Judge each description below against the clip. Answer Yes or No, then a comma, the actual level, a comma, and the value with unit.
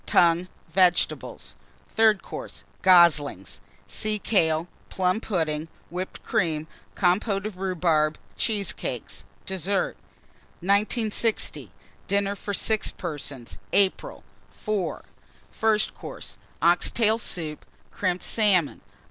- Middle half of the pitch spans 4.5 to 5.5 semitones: No, average, 3.9 semitones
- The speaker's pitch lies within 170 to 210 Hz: Yes, medium, 185 Hz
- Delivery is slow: Yes, slow, 95 wpm